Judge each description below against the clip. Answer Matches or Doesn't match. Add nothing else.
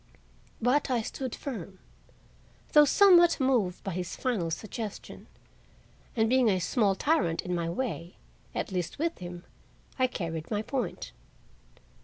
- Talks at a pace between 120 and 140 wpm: Matches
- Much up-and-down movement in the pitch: Matches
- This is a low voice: Doesn't match